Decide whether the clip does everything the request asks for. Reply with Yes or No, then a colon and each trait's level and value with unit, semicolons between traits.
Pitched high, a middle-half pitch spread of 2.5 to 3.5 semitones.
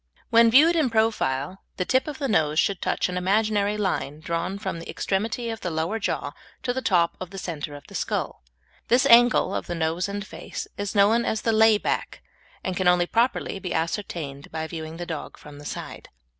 No: high, 195 Hz; average, 5.1 semitones